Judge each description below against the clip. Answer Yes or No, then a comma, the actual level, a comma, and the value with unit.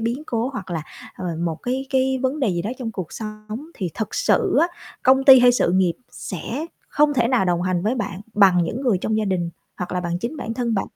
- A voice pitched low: No, high, 220 Hz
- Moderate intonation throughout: No, wide, 5.9 semitones